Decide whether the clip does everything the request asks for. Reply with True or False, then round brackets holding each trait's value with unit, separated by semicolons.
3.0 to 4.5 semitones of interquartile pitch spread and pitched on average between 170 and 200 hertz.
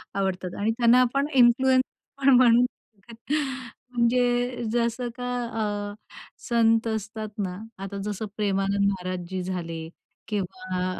False (4.2 semitones; 220 Hz)